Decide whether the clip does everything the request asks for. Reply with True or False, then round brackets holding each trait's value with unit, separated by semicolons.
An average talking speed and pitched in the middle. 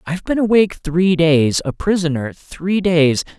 True (160 wpm; 170 Hz)